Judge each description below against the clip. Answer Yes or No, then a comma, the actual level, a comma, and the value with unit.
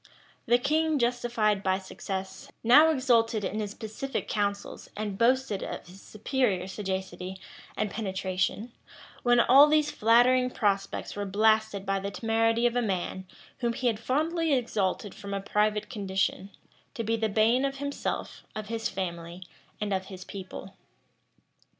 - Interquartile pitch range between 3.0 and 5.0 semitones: Yes, average, 3.8 semitones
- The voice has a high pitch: Yes, high, 215 Hz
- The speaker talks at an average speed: Yes, average, 150 wpm